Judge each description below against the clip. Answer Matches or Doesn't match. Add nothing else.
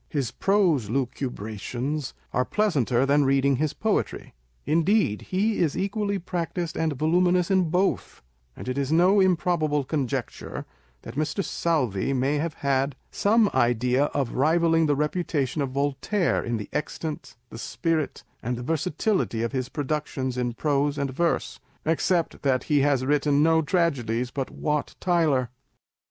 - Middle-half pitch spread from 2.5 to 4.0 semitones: Doesn't match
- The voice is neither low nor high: Matches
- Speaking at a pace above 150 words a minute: Doesn't match